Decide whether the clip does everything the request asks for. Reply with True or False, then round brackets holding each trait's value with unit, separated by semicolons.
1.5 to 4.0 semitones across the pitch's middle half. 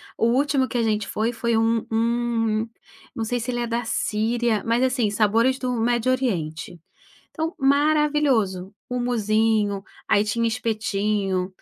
True (2.5 semitones)